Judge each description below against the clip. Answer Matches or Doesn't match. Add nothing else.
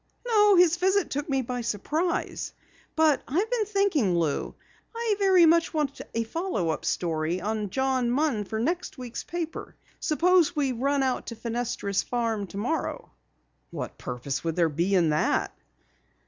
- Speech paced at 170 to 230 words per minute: Doesn't match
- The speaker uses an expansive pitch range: Matches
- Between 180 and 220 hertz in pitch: Doesn't match